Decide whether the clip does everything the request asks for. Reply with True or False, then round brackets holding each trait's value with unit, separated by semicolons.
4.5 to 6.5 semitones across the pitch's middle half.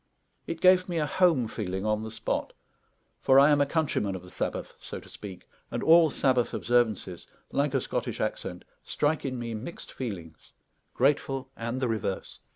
True (5.4 semitones)